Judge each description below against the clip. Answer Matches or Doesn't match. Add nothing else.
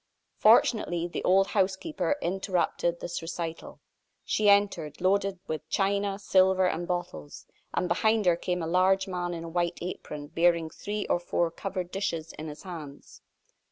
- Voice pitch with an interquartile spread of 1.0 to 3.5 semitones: Matches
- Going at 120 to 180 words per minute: Matches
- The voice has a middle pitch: Matches